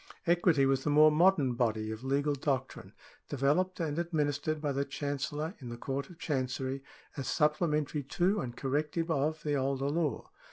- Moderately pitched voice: Yes, medium, 145 Hz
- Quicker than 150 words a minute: Yes, average, 165 wpm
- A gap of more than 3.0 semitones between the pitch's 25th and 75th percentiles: No, narrow, 2.5 semitones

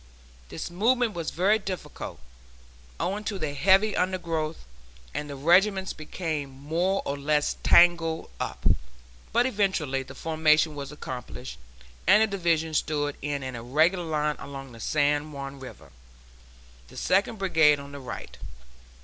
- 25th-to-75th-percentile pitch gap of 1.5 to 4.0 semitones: No, average, 4.7 semitones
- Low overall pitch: No, medium, 155 Hz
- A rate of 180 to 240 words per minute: No, average, 140 wpm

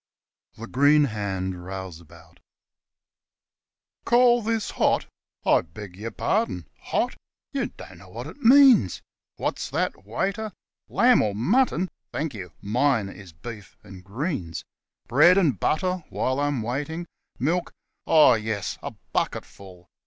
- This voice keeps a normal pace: No, slow, 130 wpm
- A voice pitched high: No, low, 120 Hz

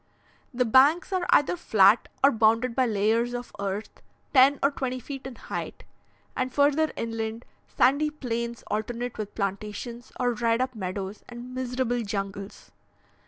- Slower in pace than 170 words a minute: Yes, average, 145 wpm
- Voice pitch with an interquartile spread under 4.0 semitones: Yes, average, 3.0 semitones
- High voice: Yes, high, 240 Hz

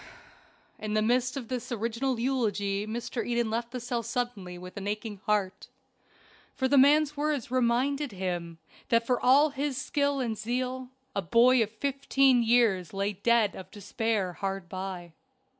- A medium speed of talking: Yes, average, 160 wpm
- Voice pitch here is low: No, high, 235 Hz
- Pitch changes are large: No, average, 4.2 semitones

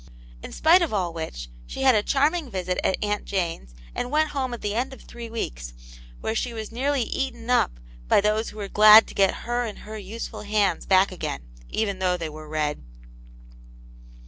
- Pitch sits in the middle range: No, high, 215 Hz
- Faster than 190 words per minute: Yes, average, 200 wpm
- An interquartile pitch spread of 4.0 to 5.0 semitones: Yes, average, 4.6 semitones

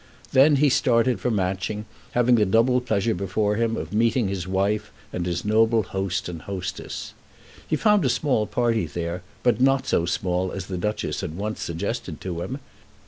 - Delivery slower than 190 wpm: Yes, average, 180 wpm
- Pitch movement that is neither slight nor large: Yes, average, 4.2 semitones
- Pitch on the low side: Yes, low, 105 Hz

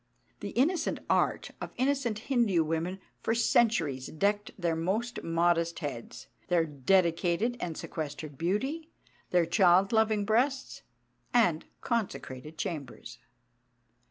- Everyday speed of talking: No, slow, 110 wpm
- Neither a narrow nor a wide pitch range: No, wide, 5.8 semitones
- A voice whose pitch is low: No, medium, 185 Hz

